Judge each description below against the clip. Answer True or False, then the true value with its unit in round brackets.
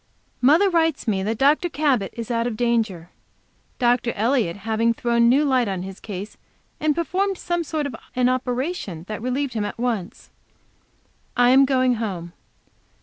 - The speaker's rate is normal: True (160 wpm)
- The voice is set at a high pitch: True (245 Hz)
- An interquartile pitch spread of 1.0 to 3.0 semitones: False (4.5 semitones)